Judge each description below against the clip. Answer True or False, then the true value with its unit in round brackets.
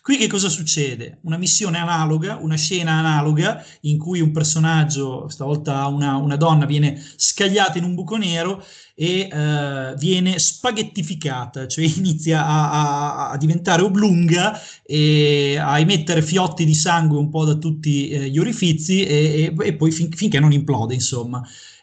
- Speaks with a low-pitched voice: False (160 Hz)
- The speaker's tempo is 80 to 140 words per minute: False (155 wpm)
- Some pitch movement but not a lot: True (3.3 semitones)